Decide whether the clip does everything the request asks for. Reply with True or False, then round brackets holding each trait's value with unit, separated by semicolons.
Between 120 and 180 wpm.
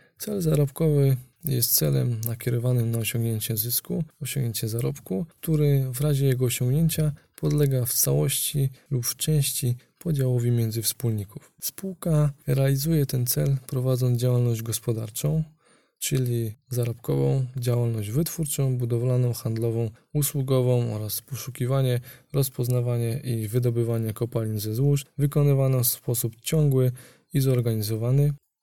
False (110 wpm)